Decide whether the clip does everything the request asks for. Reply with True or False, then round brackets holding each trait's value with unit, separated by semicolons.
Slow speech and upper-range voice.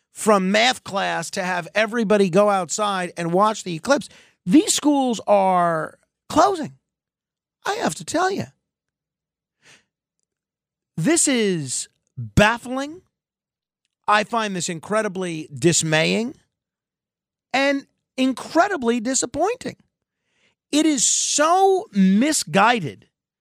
True (90 wpm; 210 Hz)